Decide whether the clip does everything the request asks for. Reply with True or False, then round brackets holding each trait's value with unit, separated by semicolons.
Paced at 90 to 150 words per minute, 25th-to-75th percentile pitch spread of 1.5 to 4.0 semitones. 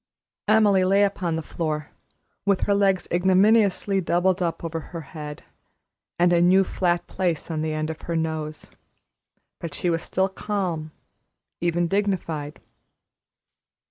True (140 wpm; 3.1 semitones)